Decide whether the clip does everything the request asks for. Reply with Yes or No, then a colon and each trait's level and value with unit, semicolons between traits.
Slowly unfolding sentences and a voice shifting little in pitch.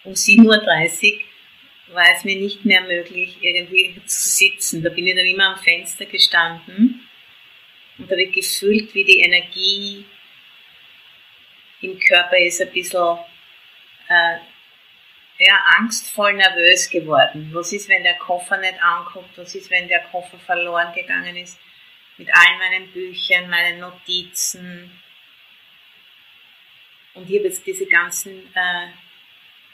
Yes: slow, 130 wpm; narrow, 2.0 semitones